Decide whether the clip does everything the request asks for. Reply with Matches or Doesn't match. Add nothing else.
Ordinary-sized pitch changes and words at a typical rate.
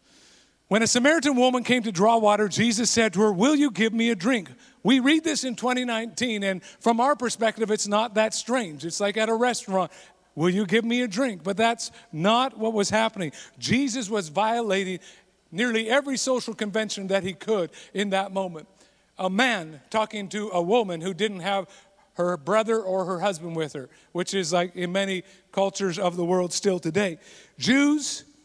Matches